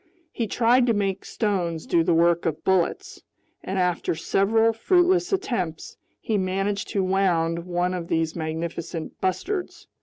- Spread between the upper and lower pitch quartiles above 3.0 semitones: Yes, average, 4.8 semitones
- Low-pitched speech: No, medium, 185 Hz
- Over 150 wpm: No, average, 145 wpm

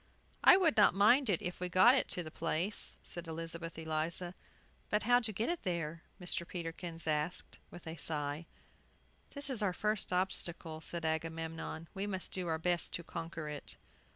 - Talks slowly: No, average, 175 wpm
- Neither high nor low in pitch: Yes, medium, 170 Hz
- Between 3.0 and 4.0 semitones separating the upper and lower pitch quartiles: Yes, average, 3.3 semitones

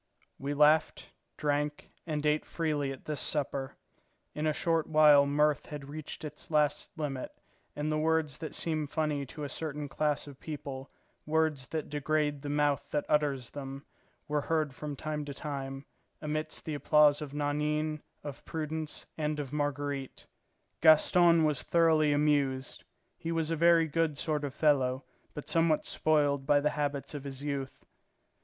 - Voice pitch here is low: No, medium, 150 Hz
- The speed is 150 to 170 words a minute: Yes, average, 160 wpm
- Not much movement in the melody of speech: Yes, narrow, 1.4 semitones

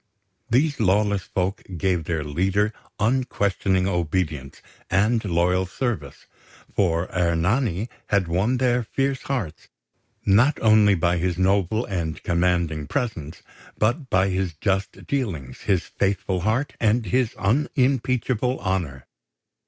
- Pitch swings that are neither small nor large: Yes, average, 4.9 semitones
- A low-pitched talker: Yes, very low, 95 Hz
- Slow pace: Yes, slow, 115 wpm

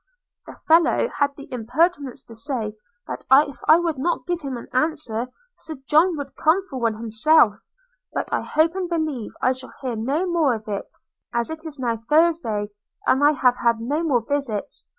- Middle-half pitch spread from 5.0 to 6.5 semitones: Yes, average, 5.3 semitones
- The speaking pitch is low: No, very high, 280 Hz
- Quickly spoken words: No, average, 190 wpm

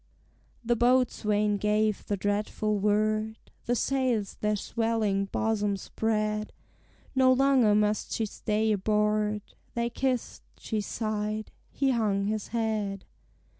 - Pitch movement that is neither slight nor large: No, narrow, 1.5 semitones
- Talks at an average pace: No, slow, 115 wpm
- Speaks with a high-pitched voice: Yes, high, 215 Hz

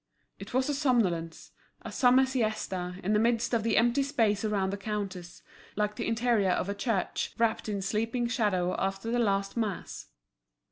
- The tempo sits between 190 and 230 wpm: No, average, 175 wpm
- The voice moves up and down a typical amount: Yes, average, 3.3 semitones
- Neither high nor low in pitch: No, high, 215 Hz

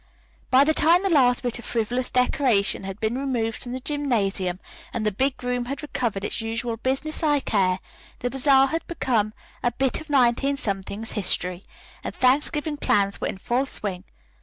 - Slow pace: No, average, 180 wpm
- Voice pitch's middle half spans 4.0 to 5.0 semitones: Yes, average, 4.4 semitones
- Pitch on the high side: Yes, high, 245 Hz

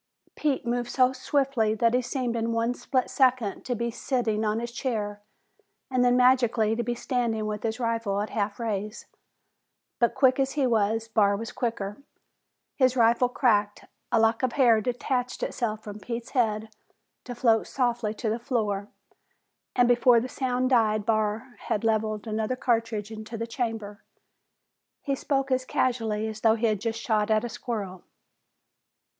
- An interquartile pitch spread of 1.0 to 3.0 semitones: Yes, narrow, 2.4 semitones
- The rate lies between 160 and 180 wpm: Yes, average, 165 wpm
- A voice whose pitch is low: No, high, 230 Hz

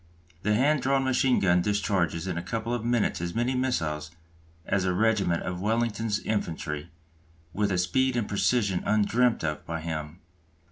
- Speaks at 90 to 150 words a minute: No, average, 160 wpm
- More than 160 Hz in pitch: No, low, 105 Hz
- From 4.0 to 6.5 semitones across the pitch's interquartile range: Yes, average, 5.3 semitones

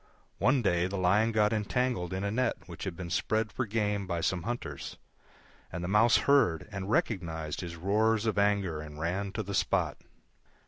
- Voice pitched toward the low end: Yes, low, 100 Hz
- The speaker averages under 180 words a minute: No, average, 185 wpm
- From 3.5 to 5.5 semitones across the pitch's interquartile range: Yes, average, 3.9 semitones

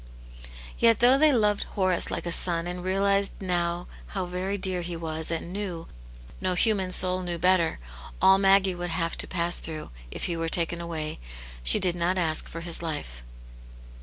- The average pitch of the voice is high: No, medium, 180 Hz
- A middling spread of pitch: No, narrow, 2.2 semitones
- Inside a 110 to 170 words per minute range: No, average, 185 wpm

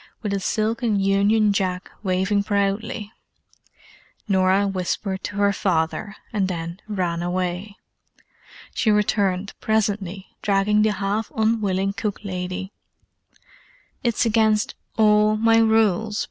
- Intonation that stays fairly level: Yes, narrow, 2.1 semitones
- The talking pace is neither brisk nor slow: No, slow, 110 wpm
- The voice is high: Yes, high, 200 Hz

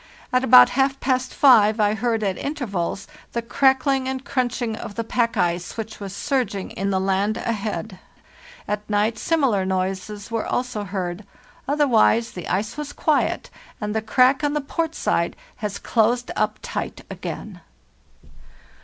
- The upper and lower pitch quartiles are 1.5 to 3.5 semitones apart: No, average, 4.0 semitones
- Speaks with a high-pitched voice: Yes, high, 225 Hz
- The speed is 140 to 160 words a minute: Yes, average, 155 wpm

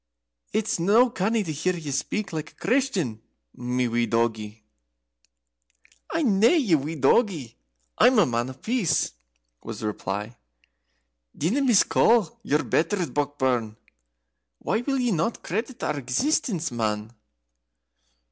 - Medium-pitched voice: Yes, medium, 160 Hz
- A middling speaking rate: No, slow, 125 wpm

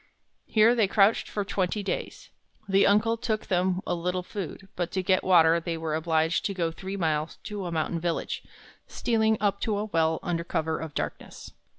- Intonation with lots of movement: No, average, 3.7 semitones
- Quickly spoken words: No, average, 190 wpm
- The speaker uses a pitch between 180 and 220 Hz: Yes, medium, 185 Hz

